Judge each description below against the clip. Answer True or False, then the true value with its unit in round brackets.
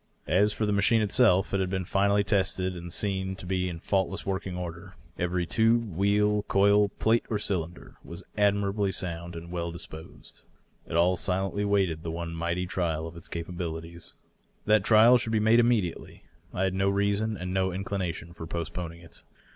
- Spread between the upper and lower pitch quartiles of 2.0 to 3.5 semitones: True (3.0 semitones)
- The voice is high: False (95 Hz)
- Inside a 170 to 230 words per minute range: True (180 wpm)